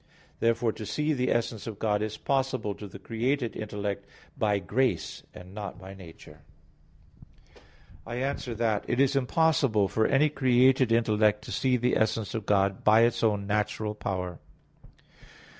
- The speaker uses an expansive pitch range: No, average, 3.5 semitones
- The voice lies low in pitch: Yes, low, 110 Hz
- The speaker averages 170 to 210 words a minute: No, average, 160 wpm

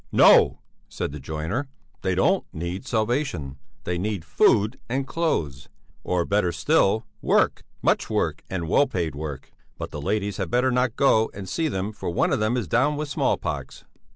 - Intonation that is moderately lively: No, wide, 7.0 semitones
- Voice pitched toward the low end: Yes, low, 105 Hz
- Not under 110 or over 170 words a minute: No, average, 180 wpm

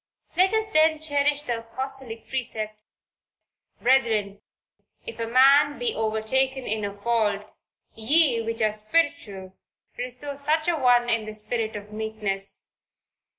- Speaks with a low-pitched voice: No, high, 235 Hz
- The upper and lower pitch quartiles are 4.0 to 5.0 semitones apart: Yes, average, 4.6 semitones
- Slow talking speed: Yes, slow, 130 wpm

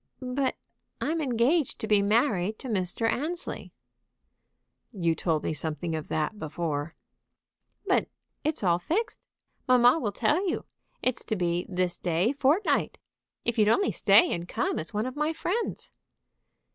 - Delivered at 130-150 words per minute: Yes, average, 145 wpm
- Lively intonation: Yes, wide, 8.5 semitones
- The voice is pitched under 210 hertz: No, high, 220 Hz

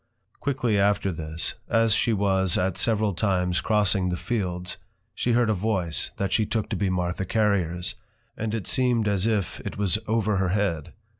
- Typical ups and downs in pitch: Yes, average, 3.3 semitones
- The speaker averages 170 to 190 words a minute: Yes, average, 175 wpm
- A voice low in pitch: Yes, low, 100 Hz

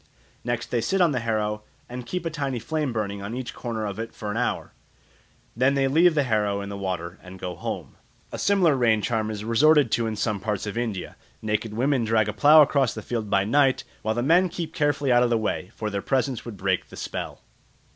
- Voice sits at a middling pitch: No, low, 115 Hz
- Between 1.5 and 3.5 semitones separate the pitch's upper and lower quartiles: No, average, 4.5 semitones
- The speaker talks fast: Yes, fast, 230 wpm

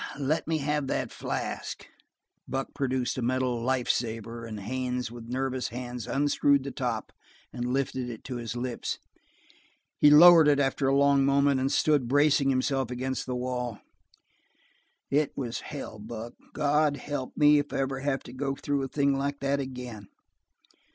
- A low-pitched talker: Yes, low, 130 Hz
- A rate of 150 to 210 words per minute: Yes, average, 165 wpm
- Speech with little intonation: Yes, narrow, 2.3 semitones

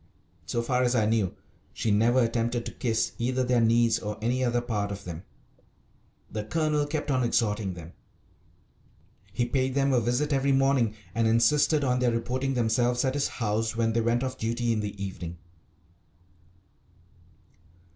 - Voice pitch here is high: No, low, 120 Hz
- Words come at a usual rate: Yes, average, 165 wpm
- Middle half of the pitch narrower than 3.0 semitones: Yes, narrow, 2.6 semitones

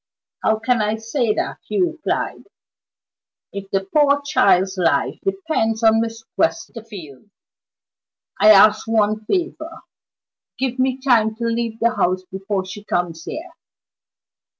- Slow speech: Yes, slow, 125 wpm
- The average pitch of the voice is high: Yes, high, 225 Hz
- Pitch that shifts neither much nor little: Yes, average, 4.5 semitones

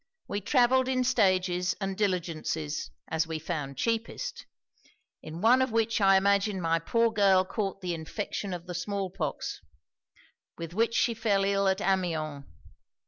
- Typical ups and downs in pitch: Yes, average, 4.3 semitones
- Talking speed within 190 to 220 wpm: No, average, 150 wpm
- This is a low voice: No, high, 195 Hz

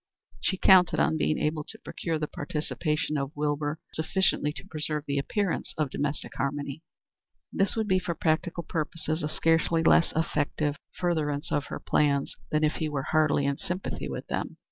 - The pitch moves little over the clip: Yes, narrow, 2.1 semitones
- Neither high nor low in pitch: Yes, medium, 155 Hz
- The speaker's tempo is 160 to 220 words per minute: Yes, average, 170 wpm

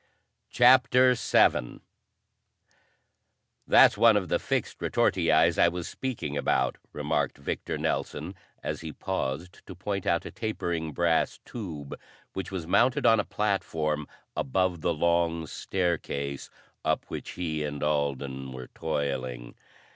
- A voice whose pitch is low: Yes, very low, 85 Hz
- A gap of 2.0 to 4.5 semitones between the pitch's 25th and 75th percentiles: No, average, 4.9 semitones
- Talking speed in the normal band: No, slow, 125 wpm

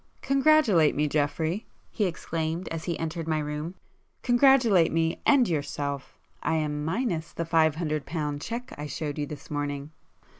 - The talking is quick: No, average, 150 wpm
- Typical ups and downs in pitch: Yes, average, 3.6 semitones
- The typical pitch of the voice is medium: Yes, medium, 160 Hz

